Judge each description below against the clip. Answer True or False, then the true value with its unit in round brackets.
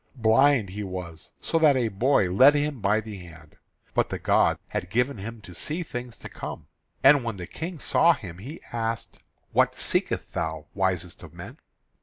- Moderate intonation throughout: False (6.8 semitones)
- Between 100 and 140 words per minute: False (185 wpm)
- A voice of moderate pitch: False (110 Hz)